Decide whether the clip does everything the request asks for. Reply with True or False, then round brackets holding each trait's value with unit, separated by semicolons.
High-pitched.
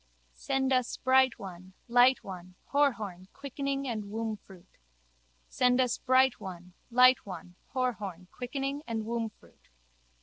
True (235 Hz)